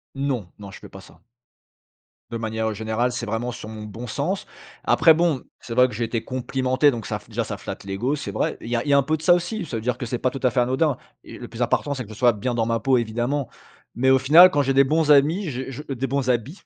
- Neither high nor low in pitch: No, low, 125 Hz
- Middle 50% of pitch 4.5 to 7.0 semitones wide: No, average, 3.5 semitones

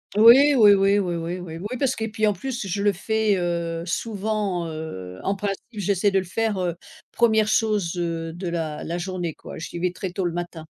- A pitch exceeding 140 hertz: Yes, high, 190 Hz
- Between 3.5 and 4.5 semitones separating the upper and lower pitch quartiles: Yes, average, 3.8 semitones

